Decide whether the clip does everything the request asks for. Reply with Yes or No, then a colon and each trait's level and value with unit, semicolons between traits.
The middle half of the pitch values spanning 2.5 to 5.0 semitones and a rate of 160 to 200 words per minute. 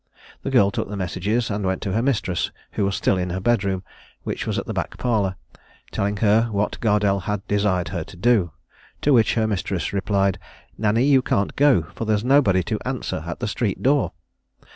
Yes: average, 3.1 semitones; average, 195 wpm